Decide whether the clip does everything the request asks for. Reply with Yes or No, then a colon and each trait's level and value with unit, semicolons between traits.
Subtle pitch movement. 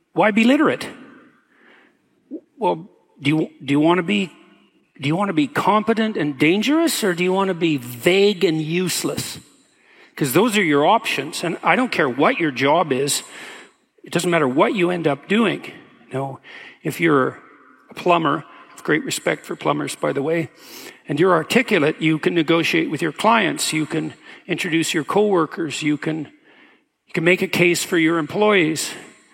No: average, 4.5 semitones